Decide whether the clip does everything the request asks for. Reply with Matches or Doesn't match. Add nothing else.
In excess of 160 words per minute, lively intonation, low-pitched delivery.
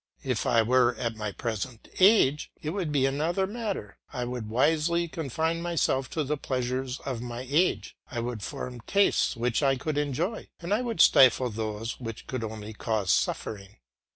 Matches